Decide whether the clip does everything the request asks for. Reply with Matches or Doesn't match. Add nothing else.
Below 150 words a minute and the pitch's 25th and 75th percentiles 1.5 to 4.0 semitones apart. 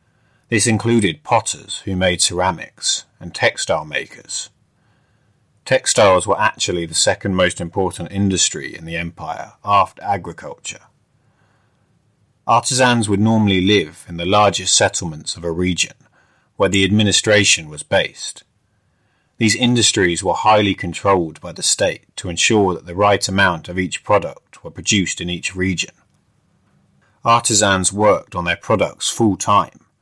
Matches